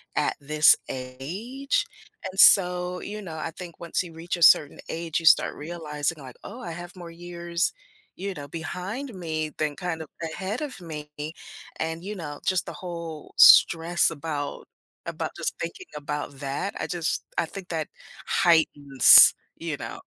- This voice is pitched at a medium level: Yes, medium, 165 Hz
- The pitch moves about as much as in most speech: Yes, average, 3.0 semitones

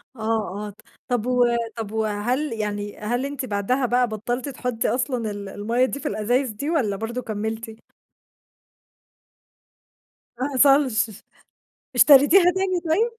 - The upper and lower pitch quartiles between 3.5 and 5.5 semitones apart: Yes, average, 4.0 semitones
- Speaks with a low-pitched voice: No, high, 245 Hz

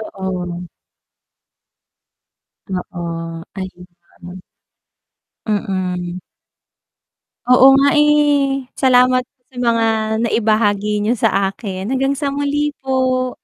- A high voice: Yes, high, 235 Hz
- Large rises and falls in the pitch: Yes, wide, 5.9 semitones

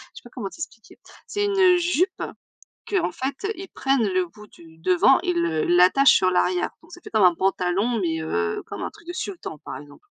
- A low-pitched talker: No, high, 205 Hz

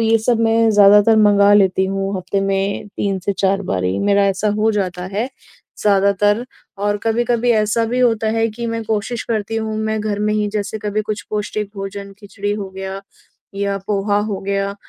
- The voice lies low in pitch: No, high, 205 Hz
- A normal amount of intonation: No, narrow, 1.8 semitones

